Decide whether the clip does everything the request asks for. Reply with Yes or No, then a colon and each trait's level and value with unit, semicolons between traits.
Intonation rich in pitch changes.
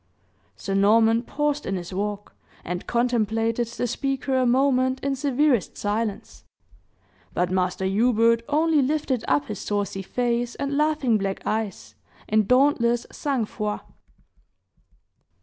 No: average, 4.4 semitones